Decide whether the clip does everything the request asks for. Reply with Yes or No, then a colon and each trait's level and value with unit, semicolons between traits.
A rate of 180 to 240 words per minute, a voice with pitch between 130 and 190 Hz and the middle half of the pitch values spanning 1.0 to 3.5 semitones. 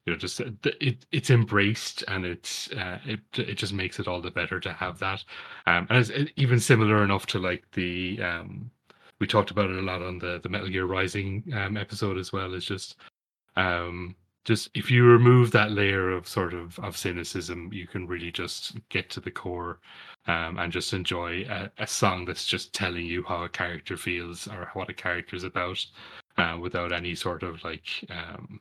No: average, 200 wpm; very low, 95 Hz; average, 2.9 semitones